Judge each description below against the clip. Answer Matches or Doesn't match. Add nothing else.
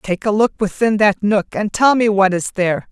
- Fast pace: Matches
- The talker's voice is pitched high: Matches